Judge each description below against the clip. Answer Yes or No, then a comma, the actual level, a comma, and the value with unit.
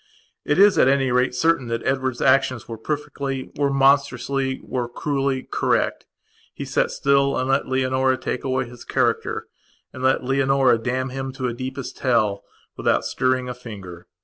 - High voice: No, low, 130 Hz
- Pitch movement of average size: No, narrow, 1.6 semitones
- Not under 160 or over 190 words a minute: No, average, 150 wpm